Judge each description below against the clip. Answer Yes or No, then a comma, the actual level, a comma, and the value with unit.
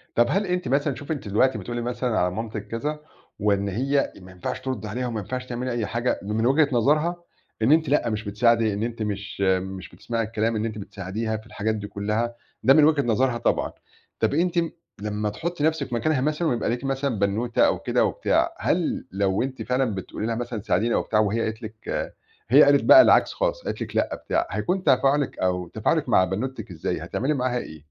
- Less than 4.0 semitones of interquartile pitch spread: No, average, 4.3 semitones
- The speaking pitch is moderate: No, low, 120 Hz